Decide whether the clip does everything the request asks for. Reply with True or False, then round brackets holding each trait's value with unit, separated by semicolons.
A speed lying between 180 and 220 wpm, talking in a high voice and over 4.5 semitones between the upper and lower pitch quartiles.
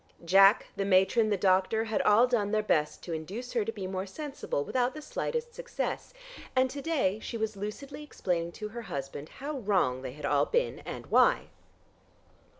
True (185 wpm; 210 Hz; 5.3 semitones)